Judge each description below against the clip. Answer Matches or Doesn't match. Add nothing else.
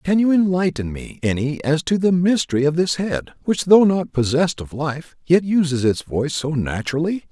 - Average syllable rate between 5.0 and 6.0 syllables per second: Matches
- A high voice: Doesn't match